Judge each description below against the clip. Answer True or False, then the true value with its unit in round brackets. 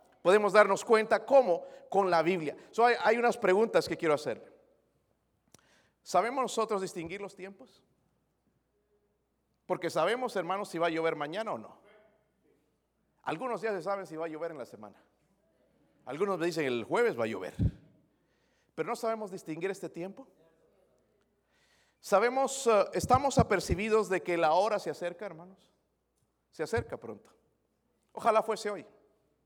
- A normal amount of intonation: True (4.5 semitones)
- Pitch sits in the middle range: False (205 Hz)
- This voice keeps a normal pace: True (145 wpm)